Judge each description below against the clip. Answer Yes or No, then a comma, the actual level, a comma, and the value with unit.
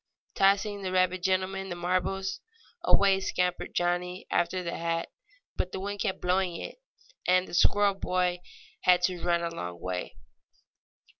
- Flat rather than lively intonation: Yes, narrow, 1.6 semitones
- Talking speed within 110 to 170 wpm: Yes, average, 155 wpm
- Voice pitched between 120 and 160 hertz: No, medium, 185 Hz